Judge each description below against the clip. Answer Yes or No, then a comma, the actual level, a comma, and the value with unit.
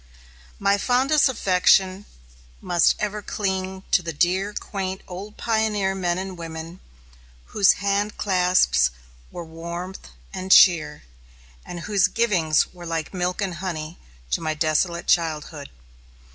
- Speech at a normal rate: No, slow, 125 wpm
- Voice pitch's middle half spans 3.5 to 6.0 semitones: No, average, 2.8 semitones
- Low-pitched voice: No, medium, 185 Hz